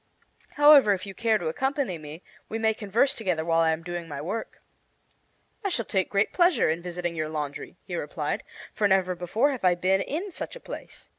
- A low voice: No, high, 190 Hz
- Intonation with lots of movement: Yes, wide, 5.7 semitones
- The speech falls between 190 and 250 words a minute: Yes, fast, 205 wpm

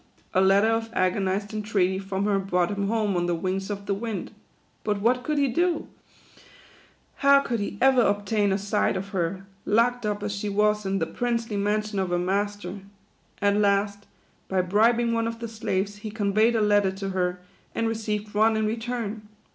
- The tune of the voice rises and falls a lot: No, narrow, 2.5 semitones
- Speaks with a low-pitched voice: No, high, 205 Hz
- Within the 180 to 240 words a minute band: Yes, average, 185 wpm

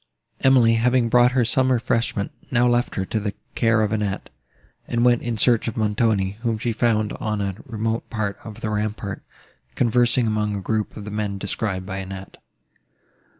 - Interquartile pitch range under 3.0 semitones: Yes, narrow, 2.4 semitones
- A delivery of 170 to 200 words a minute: Yes, average, 180 wpm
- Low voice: Yes, low, 110 Hz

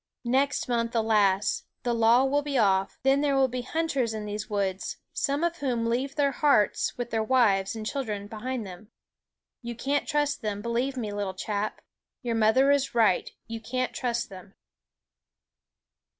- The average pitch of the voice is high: Yes, high, 235 Hz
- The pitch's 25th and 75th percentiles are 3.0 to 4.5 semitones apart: Yes, average, 4.2 semitones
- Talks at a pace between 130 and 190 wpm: Yes, average, 165 wpm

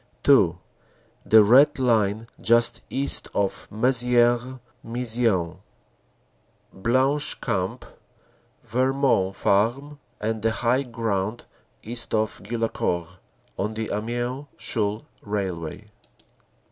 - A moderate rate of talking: No, slow, 90 wpm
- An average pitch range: Yes, average, 3.1 semitones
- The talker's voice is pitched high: No, low, 115 Hz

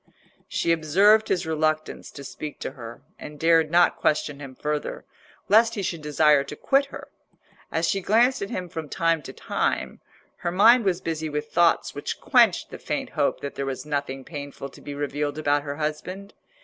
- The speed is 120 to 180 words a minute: No, average, 190 wpm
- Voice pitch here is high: No, medium, 155 Hz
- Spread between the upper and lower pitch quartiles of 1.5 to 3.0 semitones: No, average, 3.6 semitones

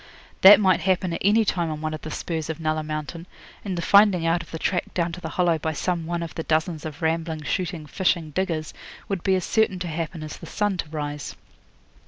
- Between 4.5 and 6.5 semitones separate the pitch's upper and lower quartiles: No, average, 2.8 semitones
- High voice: No, medium, 165 Hz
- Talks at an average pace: No, fast, 235 wpm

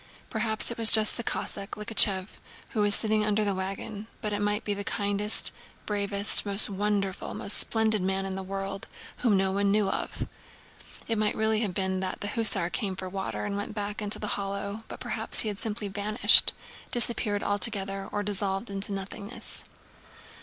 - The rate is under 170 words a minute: No, average, 180 wpm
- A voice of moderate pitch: No, high, 205 Hz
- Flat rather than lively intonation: Yes, narrow, 1.5 semitones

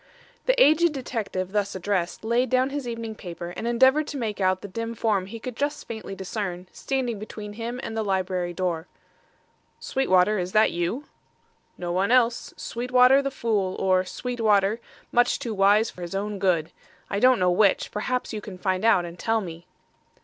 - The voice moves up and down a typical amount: Yes, average, 4.5 semitones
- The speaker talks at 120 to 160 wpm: No, average, 180 wpm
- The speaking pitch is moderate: No, high, 210 Hz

